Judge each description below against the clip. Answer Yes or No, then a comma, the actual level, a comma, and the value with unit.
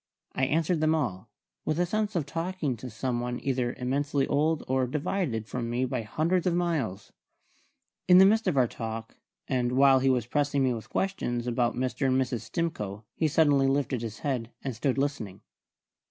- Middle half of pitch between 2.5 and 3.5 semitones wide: No, average, 4.4 semitones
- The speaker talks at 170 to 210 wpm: Yes, average, 185 wpm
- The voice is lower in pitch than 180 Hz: Yes, low, 135 Hz